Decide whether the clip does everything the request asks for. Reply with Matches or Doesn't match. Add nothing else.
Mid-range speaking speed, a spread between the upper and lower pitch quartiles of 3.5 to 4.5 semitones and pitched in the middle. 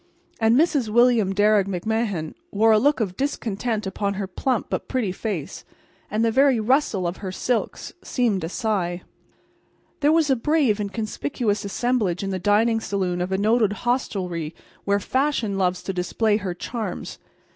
Doesn't match